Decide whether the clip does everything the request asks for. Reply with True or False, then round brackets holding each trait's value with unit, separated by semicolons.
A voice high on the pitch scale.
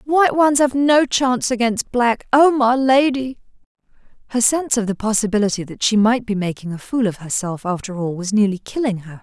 True (230 Hz)